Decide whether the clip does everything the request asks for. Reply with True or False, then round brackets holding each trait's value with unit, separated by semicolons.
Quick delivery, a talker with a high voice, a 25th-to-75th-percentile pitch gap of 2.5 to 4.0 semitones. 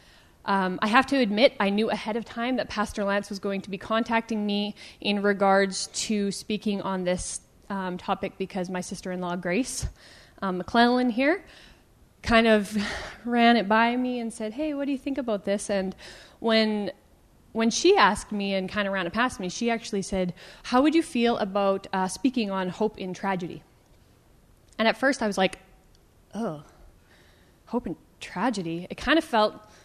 False (185 wpm; 210 Hz; 3.3 semitones)